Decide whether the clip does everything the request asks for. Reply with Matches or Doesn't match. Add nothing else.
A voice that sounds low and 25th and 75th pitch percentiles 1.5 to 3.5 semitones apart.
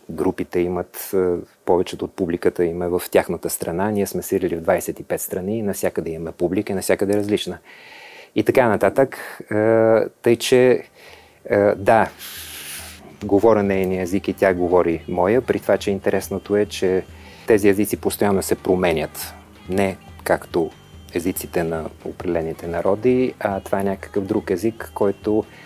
Matches